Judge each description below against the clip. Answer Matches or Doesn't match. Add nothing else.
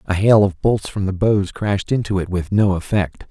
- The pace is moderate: Doesn't match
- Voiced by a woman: Doesn't match